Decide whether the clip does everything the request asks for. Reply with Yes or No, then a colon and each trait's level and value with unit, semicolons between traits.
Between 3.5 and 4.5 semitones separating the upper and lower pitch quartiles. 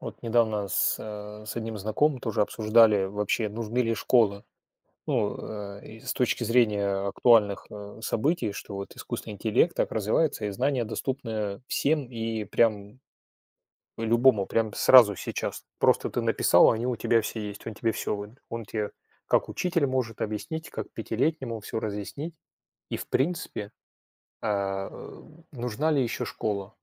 No: average, 2.9 semitones